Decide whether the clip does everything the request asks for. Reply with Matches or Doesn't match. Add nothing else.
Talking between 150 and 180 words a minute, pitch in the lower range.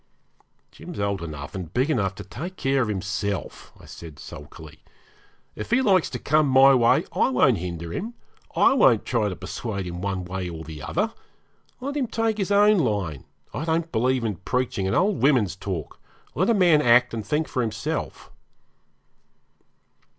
Matches